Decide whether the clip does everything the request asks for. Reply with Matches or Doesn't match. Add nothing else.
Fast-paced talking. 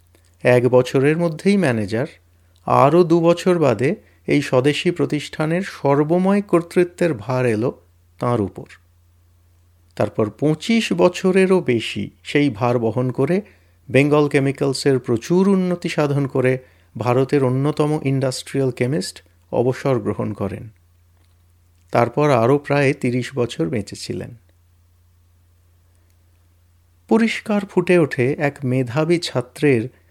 Doesn't match